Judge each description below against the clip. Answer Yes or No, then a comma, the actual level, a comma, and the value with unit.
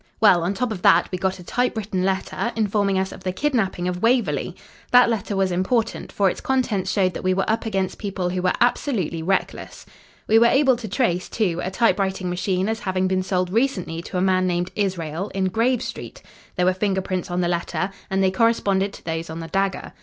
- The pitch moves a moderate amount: Yes, average, 3.2 semitones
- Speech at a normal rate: No, fast, 215 wpm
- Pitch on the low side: No, high, 190 Hz